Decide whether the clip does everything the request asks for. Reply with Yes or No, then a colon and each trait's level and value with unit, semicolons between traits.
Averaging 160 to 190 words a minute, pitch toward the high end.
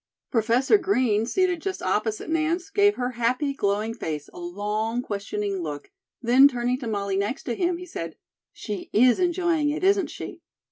Yes: average, 170 wpm; high, 245 Hz